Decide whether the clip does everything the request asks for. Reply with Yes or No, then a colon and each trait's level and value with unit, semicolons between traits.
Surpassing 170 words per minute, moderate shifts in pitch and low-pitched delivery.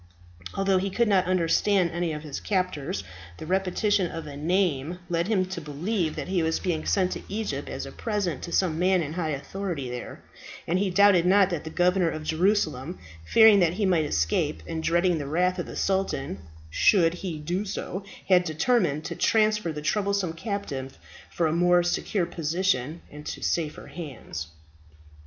No: average, 180 wpm; average, 3.5 semitones; medium, 175 Hz